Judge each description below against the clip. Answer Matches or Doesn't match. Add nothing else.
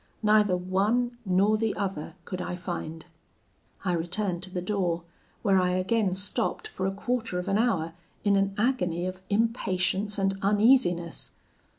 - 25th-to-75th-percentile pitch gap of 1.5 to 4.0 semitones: Matches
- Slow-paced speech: Doesn't match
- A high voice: Matches